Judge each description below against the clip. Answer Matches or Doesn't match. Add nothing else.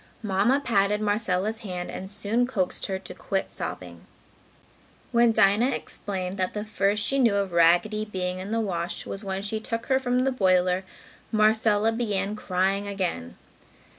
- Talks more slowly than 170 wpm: Matches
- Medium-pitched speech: Doesn't match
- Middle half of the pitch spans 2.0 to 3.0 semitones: Matches